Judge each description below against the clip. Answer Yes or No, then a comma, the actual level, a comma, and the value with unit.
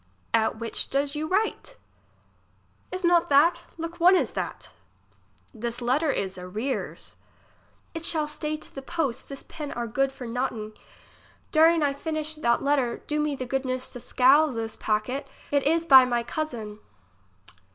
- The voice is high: Yes, very high, 275 Hz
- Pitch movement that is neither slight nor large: Yes, average, 4.5 semitones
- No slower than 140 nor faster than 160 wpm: Yes, average, 155 wpm